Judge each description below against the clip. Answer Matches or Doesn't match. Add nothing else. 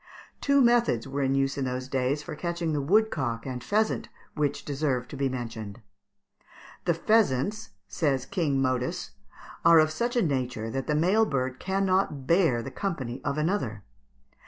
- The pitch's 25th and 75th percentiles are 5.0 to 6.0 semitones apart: Matches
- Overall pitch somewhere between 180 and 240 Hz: Doesn't match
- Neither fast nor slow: Matches